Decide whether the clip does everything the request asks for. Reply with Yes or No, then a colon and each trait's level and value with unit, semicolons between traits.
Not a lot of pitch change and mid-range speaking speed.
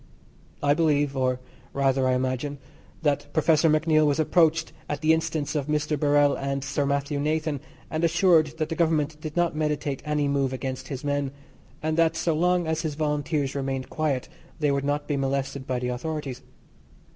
Yes: narrow, 2.2 semitones; average, 180 wpm